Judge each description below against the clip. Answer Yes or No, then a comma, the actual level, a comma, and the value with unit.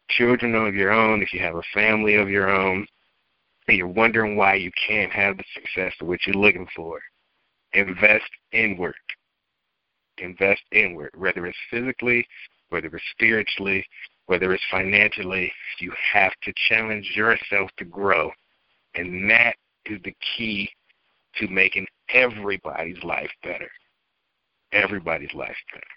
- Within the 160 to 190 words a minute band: No, slow, 135 wpm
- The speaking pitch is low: Yes, low, 100 Hz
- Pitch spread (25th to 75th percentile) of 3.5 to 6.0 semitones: No, average, 2.7 semitones